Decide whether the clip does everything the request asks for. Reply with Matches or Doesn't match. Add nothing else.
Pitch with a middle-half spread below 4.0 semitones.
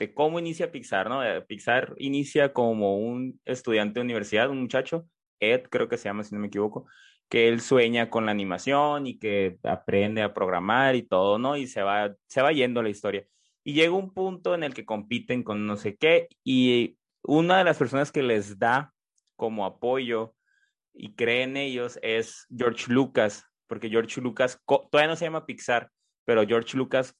Doesn't match